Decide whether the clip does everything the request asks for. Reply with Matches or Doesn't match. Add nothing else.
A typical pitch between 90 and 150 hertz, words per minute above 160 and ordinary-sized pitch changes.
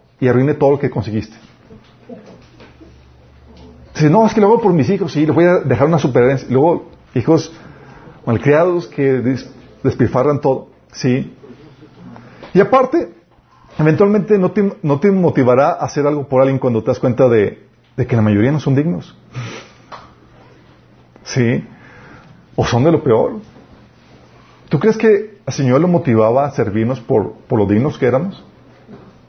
Doesn't match